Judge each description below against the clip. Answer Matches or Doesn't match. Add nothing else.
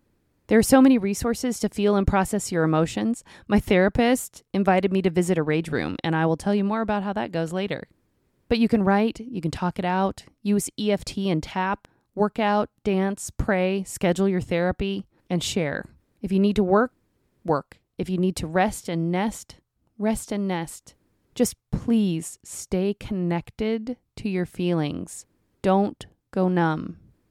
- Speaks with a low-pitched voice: Doesn't match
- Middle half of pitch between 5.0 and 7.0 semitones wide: Doesn't match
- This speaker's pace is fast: Doesn't match